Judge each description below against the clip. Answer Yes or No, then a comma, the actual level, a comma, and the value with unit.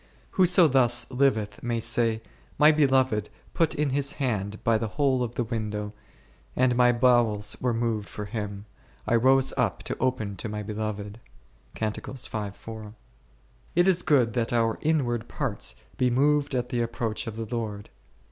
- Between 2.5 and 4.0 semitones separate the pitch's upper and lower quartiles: Yes, average, 3.4 semitones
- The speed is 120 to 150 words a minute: No, average, 160 wpm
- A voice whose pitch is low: Yes, low, 120 Hz